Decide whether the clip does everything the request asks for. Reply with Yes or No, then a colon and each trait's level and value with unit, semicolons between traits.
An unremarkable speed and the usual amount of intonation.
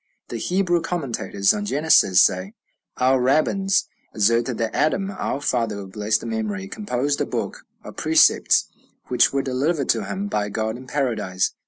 No: average, 155 wpm; wide, 6.6 semitones